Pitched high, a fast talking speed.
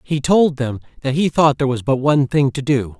No: medium, 140 Hz; fast, 260 wpm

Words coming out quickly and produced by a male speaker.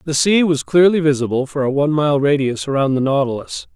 Yes: fast, 210 wpm; male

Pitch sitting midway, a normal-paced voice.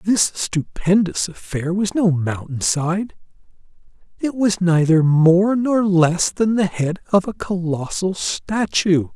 No: medium, 180 Hz; slow, 125 wpm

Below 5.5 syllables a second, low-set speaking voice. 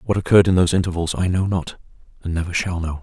No: 7.0 syllables/s; very low, 90 Hz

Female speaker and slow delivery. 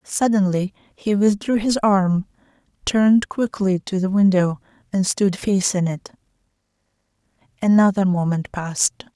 Yes: female; slow, 110 wpm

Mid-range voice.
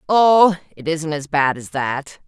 Yes: medium, 160 Hz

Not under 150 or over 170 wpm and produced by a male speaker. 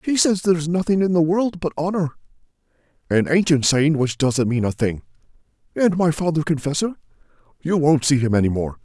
No: average, 185 wpm; male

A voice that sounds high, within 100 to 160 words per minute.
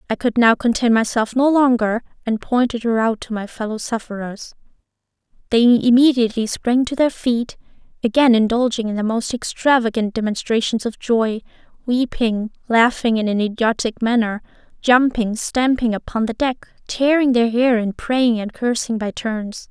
Yes: high, 230 Hz; average, 150 wpm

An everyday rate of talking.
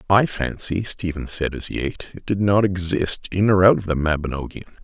No: fast, 210 wpm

